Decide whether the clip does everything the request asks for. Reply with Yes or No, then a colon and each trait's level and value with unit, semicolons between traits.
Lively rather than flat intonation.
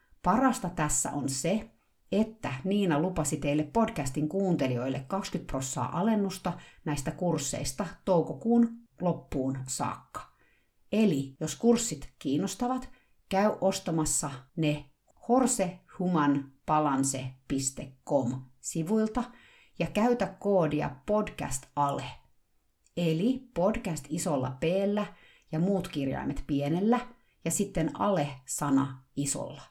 Yes: wide, 5.9 semitones